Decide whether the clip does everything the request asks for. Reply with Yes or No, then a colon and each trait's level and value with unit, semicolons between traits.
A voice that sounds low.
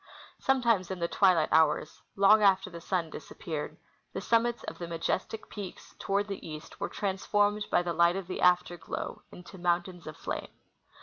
No: medium, 185 Hz